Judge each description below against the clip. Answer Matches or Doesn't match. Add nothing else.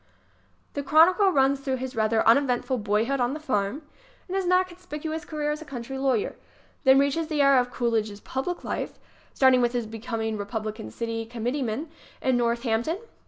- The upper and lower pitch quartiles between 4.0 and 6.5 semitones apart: Matches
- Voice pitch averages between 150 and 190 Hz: Doesn't match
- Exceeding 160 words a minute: Matches